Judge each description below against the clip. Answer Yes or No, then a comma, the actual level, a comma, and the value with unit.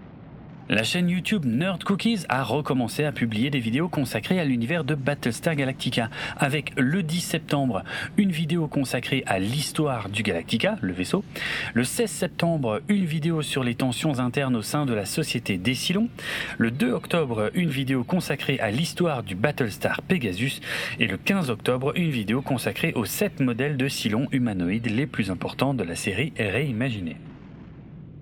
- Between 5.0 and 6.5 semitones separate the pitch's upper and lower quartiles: Yes, average, 5.3 semitones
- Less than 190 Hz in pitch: Yes, medium, 140 Hz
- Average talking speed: Yes, average, 165 wpm